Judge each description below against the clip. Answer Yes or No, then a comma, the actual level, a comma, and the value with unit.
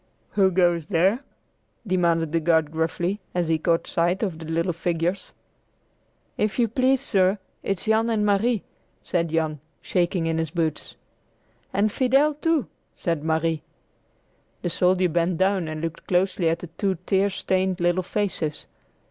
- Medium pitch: Yes, medium, 180 Hz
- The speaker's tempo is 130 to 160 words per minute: Yes, average, 150 wpm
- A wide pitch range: No, average, 3.3 semitones